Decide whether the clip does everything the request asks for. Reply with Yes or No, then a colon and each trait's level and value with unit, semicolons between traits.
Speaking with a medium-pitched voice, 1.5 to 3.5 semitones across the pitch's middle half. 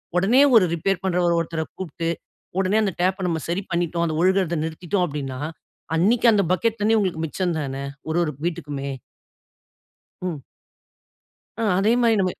Yes: medium, 175 Hz; average, 3.1 semitones